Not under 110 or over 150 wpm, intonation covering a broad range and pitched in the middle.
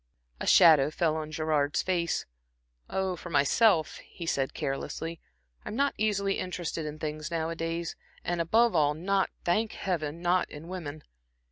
No: average, 145 wpm; average, 3.1 semitones; medium, 165 Hz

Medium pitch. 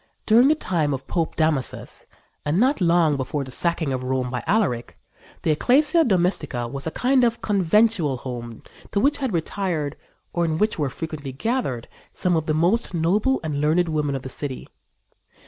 Yes: medium, 160 Hz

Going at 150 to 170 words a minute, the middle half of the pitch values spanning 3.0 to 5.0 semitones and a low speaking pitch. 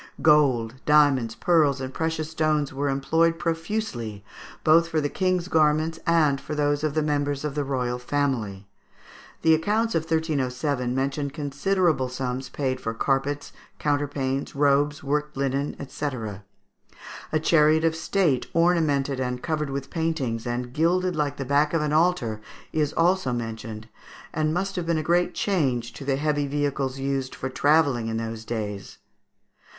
No: average, 155 wpm; average, 3.4 semitones; medium, 145 Hz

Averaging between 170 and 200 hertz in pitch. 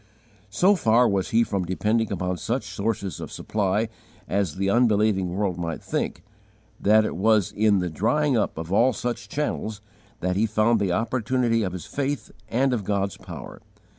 No: low, 105 Hz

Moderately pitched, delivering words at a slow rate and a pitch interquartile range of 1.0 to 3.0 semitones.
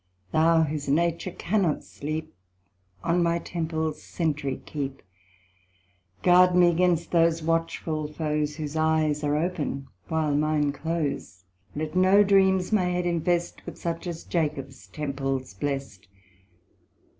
Yes: medium, 160 Hz; slow, 120 wpm; narrow, 2.6 semitones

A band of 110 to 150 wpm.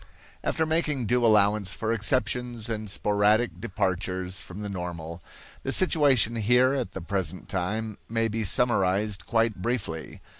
Yes: average, 140 wpm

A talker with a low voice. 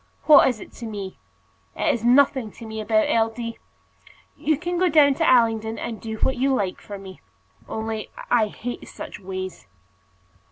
No: high, 225 Hz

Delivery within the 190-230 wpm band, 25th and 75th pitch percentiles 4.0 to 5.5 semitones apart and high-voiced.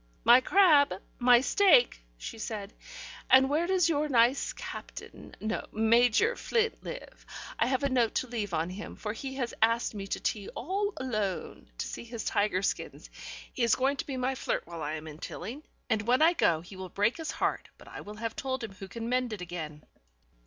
Yes: fast, 205 wpm; average, 4.6 semitones; high, 235 Hz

